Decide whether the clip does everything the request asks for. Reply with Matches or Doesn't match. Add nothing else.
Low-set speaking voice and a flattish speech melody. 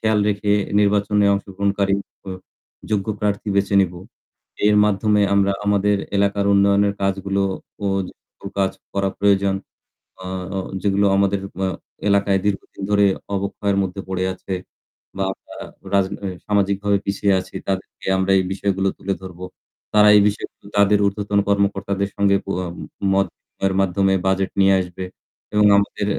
Matches